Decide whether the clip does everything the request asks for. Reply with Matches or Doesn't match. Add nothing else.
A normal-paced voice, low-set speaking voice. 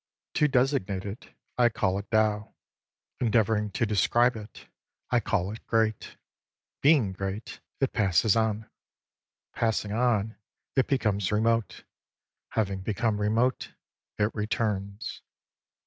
Doesn't match